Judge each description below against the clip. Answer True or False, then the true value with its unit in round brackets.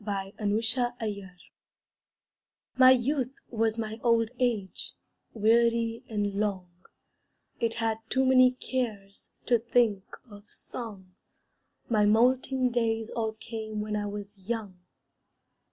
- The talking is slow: True (110 wpm)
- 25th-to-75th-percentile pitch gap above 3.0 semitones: False (2.6 semitones)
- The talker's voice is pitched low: False (225 Hz)